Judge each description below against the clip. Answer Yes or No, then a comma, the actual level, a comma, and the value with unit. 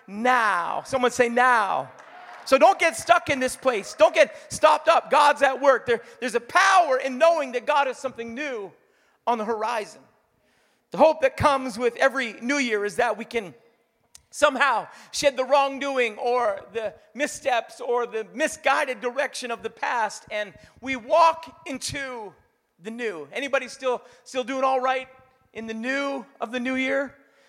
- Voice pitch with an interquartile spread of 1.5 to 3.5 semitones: Yes, average, 3.1 semitones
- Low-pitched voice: No, very high, 260 Hz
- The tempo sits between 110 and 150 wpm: No, average, 170 wpm